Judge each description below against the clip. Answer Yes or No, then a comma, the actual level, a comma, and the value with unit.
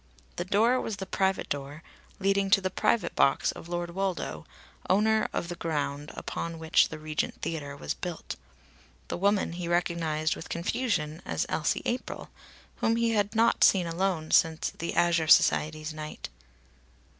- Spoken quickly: No, average, 155 wpm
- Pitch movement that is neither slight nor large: Yes, average, 3.9 semitones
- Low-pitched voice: No, medium, 170 Hz